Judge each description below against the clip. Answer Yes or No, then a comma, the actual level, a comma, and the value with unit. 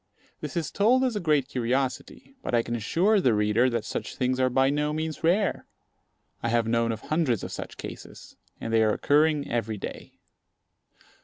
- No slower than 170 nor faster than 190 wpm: Yes, average, 185 wpm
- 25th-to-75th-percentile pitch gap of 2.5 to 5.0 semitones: No, wide, 5.4 semitones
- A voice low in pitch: Yes, low, 130 Hz